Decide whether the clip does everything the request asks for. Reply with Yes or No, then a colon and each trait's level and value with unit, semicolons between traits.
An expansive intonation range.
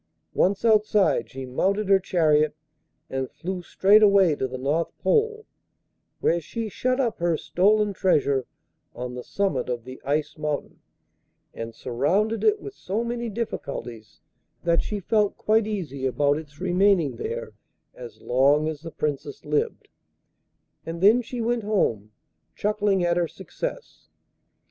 Yes: wide, 6.6 semitones